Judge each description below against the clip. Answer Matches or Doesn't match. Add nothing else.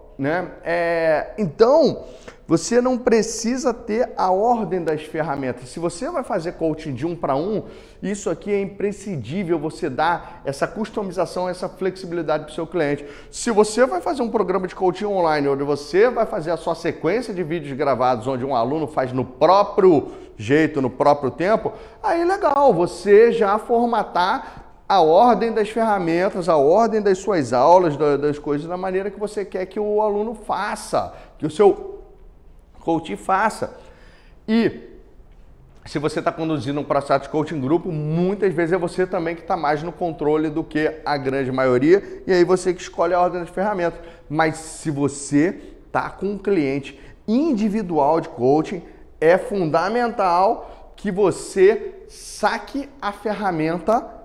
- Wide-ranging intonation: Matches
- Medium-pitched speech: Matches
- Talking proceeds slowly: Doesn't match